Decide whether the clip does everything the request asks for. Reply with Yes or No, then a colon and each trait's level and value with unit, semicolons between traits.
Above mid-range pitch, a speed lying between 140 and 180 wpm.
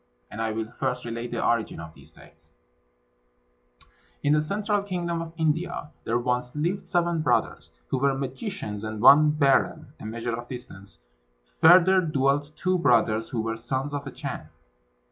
No: low, 135 Hz; average, 165 wpm